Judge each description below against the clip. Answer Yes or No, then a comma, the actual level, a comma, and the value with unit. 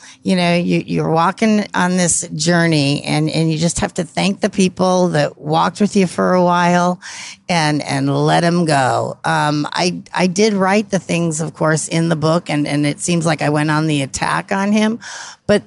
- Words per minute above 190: Yes, fast, 205 wpm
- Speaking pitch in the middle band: Yes, medium, 170 Hz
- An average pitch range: Yes, average, 3.2 semitones